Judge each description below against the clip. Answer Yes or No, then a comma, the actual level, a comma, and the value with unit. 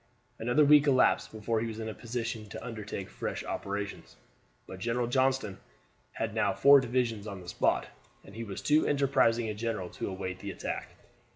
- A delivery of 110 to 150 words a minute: No, average, 180 wpm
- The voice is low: Yes, low, 115 Hz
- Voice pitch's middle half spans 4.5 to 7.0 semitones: No, average, 3.7 semitones